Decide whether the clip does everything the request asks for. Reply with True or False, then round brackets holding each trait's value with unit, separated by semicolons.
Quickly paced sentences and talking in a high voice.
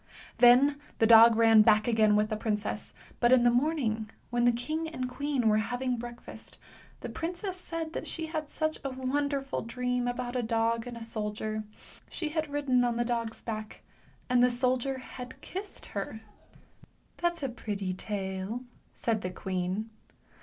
False (175 wpm; 240 Hz)